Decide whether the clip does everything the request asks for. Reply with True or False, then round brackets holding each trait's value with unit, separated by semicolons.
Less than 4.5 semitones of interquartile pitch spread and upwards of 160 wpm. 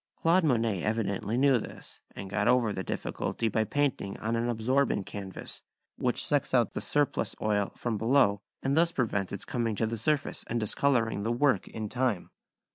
True (4.0 semitones; 180 wpm)